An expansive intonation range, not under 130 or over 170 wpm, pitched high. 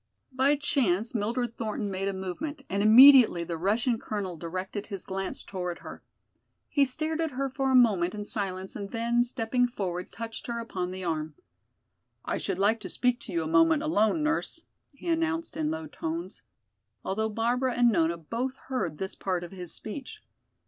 No: wide, 5.8 semitones; average, 180 wpm; high, 225 Hz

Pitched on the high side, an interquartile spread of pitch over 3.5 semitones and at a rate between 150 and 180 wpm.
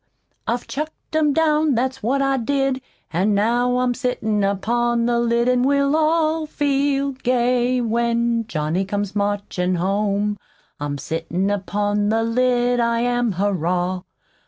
No: high, 235 Hz; average, 4.1 semitones; slow, 135 wpm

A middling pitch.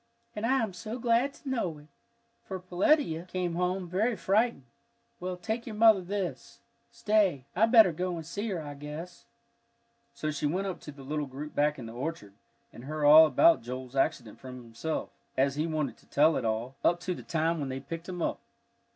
Yes: medium, 165 Hz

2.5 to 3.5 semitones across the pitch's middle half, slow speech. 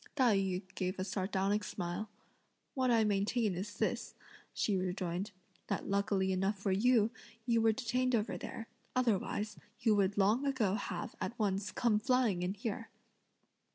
No: average, 3.2 semitones; average, 155 wpm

